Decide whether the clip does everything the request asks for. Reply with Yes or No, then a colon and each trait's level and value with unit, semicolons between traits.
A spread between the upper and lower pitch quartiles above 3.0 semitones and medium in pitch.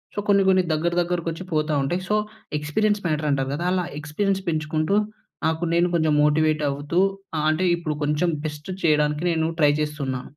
No: average, 2.7 semitones; medium, 155 Hz